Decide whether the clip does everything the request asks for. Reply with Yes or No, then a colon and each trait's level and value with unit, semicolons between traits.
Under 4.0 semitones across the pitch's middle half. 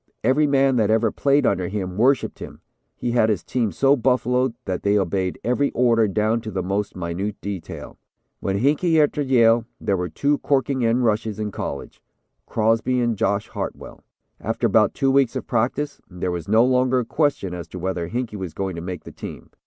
No: average, 4.9 semitones